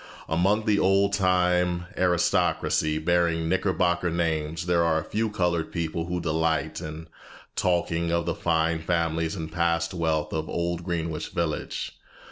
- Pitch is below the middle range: Yes, very low, 85 Hz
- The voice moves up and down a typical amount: No, narrow, 1.6 semitones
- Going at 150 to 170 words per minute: No, average, 140 wpm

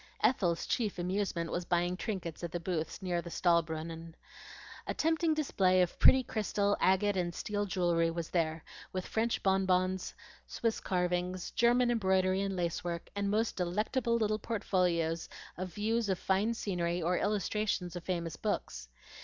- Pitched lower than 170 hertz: No, medium, 185 Hz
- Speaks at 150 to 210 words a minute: Yes, average, 155 wpm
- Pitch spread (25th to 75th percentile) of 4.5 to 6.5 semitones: No, average, 3.2 semitones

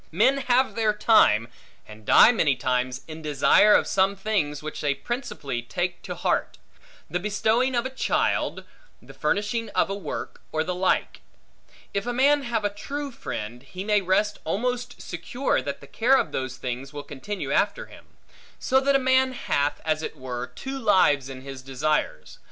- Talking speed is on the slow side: No, average, 180 wpm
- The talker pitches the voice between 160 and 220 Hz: Yes, high, 190 Hz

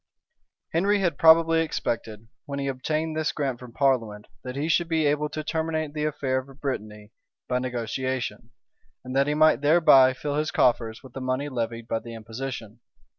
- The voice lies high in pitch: No, low, 135 Hz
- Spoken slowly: No, average, 175 wpm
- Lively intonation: No, average, 4.2 semitones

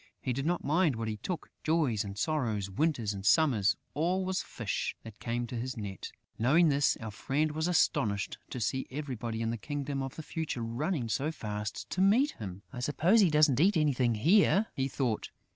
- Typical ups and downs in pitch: No, wide, 5.9 semitones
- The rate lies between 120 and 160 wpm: No, average, 195 wpm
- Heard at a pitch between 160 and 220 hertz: No, low, 135 Hz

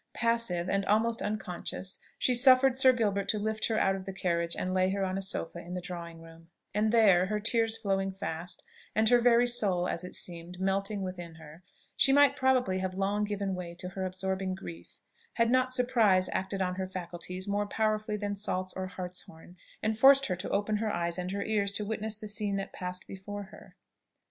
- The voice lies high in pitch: Yes, high, 195 Hz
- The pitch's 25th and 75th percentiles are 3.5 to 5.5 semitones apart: No, average, 2.9 semitones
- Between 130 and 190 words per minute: No, fast, 205 wpm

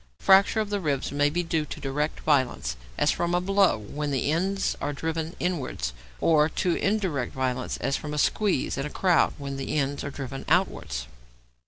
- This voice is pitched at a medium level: Yes, medium, 150 Hz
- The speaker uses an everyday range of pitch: Yes, average, 4.5 semitones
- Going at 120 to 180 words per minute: No, average, 190 wpm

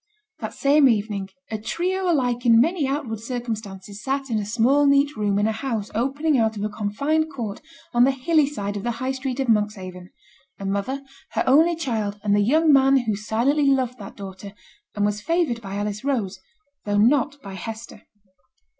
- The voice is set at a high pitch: Yes, high, 235 Hz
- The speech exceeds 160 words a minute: Yes, average, 190 wpm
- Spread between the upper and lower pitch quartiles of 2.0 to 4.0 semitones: No, average, 5.0 semitones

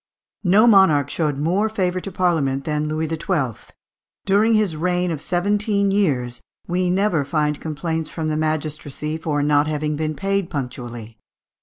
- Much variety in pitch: No, average, 3.9 semitones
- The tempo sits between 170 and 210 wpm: No, average, 150 wpm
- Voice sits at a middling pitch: Yes, medium, 160 Hz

